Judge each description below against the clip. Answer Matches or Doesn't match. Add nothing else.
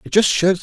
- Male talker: Matches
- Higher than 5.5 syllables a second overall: Doesn't match